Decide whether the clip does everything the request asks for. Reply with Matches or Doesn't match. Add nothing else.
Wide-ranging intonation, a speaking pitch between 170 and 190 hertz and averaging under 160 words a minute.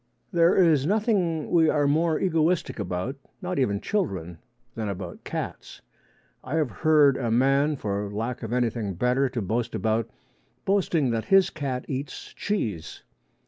Doesn't match